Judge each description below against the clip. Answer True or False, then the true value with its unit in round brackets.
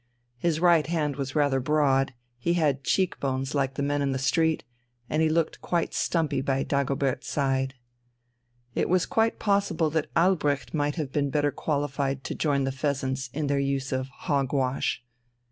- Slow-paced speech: False (175 wpm)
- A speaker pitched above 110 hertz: True (140 Hz)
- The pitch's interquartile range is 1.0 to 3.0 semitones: True (2.5 semitones)